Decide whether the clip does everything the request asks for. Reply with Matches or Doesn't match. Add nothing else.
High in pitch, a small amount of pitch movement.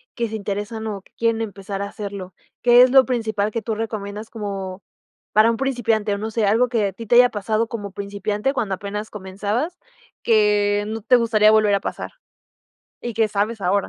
Matches